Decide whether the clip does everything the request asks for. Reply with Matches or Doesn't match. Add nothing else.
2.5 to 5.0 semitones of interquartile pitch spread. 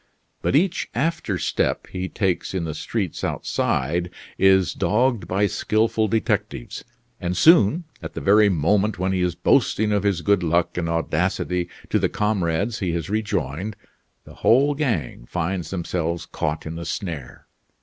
Matches